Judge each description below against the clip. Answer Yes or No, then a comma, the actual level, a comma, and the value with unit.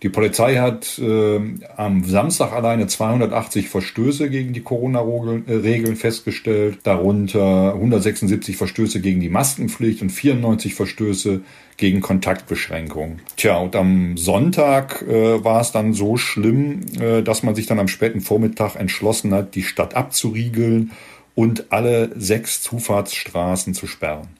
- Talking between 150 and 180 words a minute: No, average, 130 wpm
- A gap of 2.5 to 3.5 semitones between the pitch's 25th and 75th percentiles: Yes, average, 2.8 semitones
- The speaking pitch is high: No, low, 110 Hz